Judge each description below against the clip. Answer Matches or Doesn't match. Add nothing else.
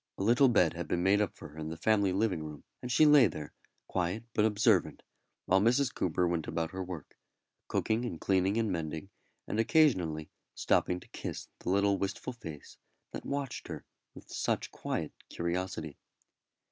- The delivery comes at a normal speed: Matches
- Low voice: Matches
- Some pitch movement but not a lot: Matches